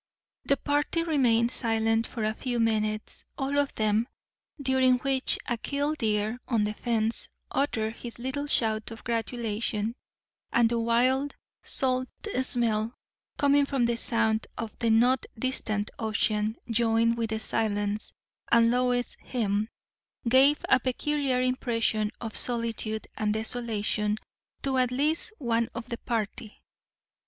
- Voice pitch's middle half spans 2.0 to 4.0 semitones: Yes, average, 2.8 semitones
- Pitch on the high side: Yes, high, 235 Hz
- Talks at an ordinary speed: No, slow, 130 wpm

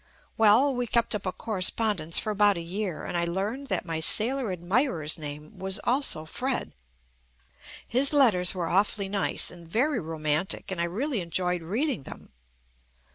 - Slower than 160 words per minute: No, average, 170 wpm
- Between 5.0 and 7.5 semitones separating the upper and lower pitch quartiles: Yes, wide, 5.5 semitones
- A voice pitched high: Yes, high, 195 Hz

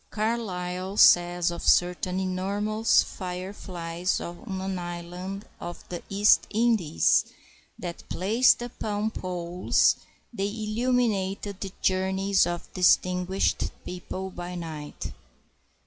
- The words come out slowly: Yes, slow, 100 wpm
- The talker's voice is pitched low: No, medium, 185 Hz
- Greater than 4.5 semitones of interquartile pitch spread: No, narrow, 2.6 semitones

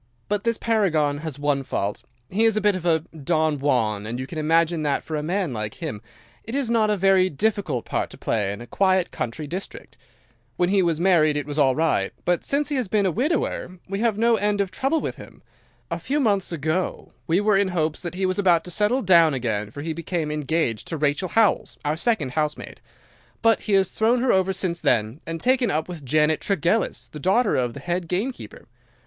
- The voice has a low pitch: No, medium, 175 Hz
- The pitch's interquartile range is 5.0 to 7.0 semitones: Yes, average, 5.3 semitones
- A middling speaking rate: No, fast, 225 wpm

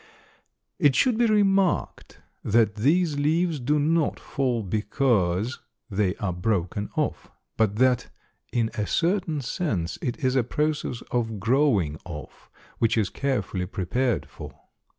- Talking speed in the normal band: No, slow, 130 wpm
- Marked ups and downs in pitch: Yes, wide, 6.5 semitones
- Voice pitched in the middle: No, low, 120 Hz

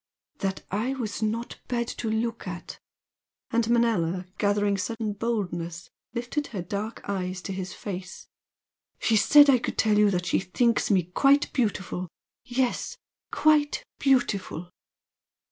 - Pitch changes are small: No, average, 4.1 semitones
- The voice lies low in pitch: No, high, 215 Hz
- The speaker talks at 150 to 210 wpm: No, average, 140 wpm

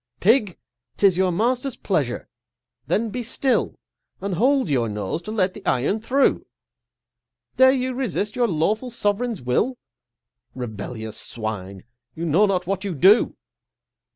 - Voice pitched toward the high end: Yes, high, 200 Hz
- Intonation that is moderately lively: No, wide, 7.9 semitones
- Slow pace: Yes, slow, 130 wpm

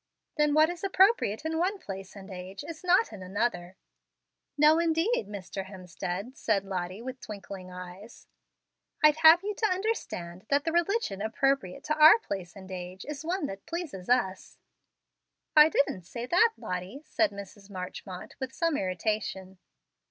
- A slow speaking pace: No, average, 155 wpm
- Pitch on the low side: No, high, 220 Hz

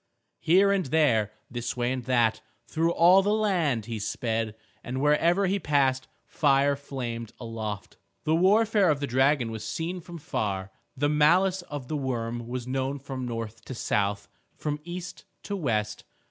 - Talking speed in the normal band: Yes, average, 160 wpm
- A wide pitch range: Yes, wide, 6.2 semitones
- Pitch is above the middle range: No, low, 135 Hz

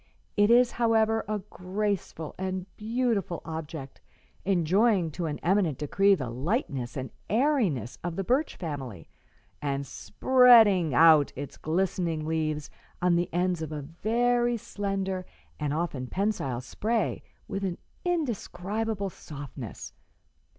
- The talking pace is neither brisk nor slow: No, slow, 120 wpm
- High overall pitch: No, medium, 180 Hz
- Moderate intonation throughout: No, wide, 5.8 semitones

